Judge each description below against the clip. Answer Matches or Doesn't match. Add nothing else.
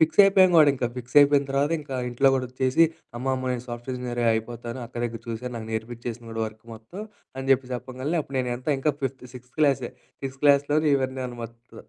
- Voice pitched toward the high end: Doesn't match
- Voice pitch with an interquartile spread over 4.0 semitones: Doesn't match